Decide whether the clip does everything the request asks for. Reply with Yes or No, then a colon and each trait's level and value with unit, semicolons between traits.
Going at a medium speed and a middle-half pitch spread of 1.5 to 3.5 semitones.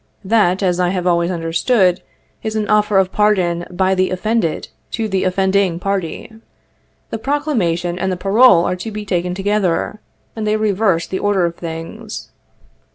Yes: average, 160 wpm; average, 3.2 semitones